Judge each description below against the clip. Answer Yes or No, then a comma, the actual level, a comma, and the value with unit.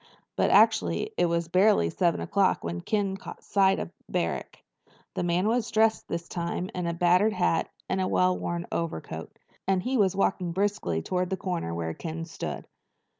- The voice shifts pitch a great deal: No, narrow, 2.5 semitones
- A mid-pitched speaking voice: Yes, medium, 180 Hz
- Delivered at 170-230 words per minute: Yes, average, 175 wpm